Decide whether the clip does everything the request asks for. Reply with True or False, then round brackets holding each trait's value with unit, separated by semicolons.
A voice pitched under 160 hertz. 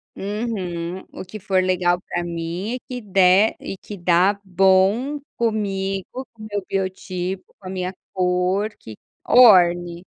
False (190 Hz)